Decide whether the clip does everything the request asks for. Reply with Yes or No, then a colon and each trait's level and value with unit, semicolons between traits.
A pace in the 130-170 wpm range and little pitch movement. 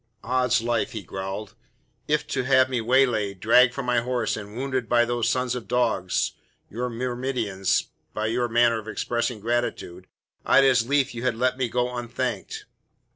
Yes: average, 165 wpm; narrow, 2.2 semitones